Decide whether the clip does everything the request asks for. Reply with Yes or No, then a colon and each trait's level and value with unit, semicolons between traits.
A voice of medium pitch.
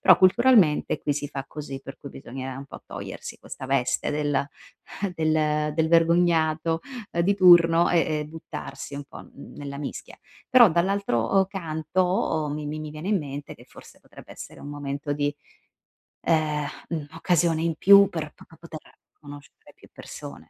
Yes: medium, 155 Hz